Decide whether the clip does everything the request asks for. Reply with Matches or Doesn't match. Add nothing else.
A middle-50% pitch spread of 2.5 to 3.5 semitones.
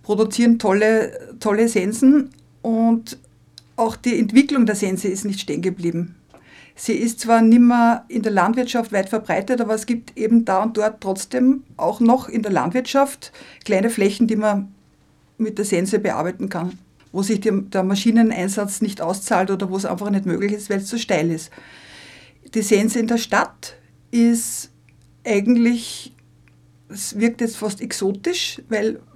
Matches